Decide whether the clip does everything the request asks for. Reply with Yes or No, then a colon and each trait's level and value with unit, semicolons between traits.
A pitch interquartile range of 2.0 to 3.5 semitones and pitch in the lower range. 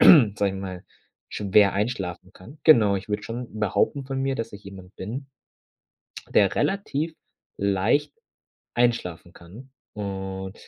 No: average, 4.6 semitones; low, 105 Hz